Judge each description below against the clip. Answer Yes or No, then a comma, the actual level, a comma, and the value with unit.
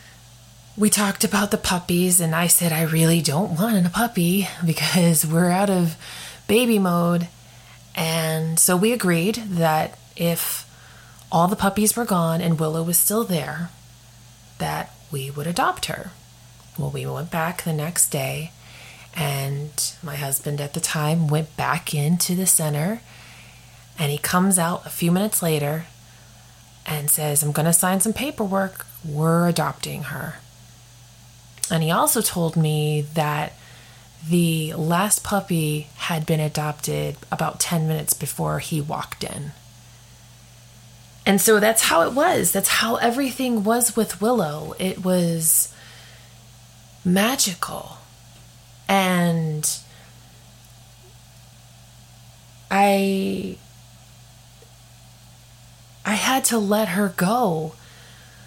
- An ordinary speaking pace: No, slow, 125 wpm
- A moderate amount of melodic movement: No, wide, 6.8 semitones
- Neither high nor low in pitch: Yes, medium, 160 Hz